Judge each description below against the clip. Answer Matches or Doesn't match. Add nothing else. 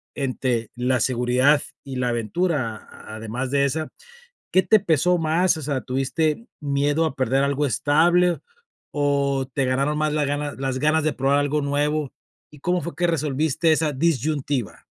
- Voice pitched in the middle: Matches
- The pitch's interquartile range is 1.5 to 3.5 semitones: Matches